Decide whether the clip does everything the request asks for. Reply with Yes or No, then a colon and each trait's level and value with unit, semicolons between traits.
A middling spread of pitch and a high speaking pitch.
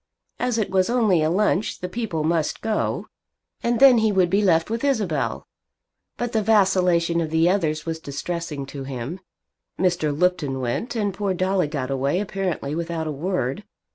No: average, 4.7 semitones; medium, 180 Hz